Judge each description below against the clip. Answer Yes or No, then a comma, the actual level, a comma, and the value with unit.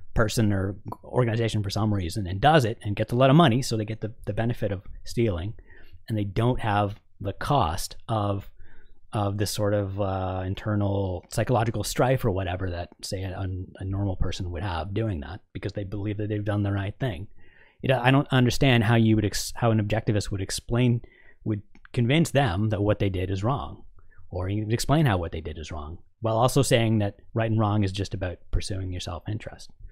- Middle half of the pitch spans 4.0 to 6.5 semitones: No, average, 3.2 semitones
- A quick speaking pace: Yes, fast, 210 wpm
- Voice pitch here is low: Yes, low, 105 Hz